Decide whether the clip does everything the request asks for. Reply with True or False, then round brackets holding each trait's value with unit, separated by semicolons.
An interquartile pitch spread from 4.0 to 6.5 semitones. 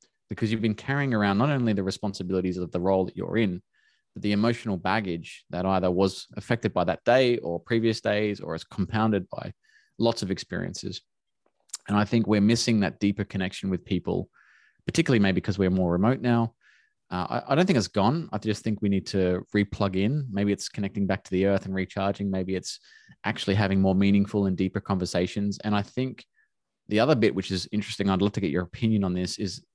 False (2.5 semitones)